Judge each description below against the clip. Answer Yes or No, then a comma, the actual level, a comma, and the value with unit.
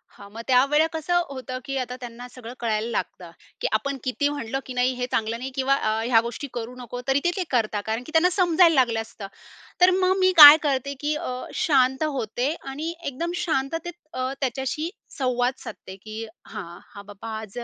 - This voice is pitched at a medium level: No, very high, 260 Hz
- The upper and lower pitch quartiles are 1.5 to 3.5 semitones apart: No, average, 4.2 semitones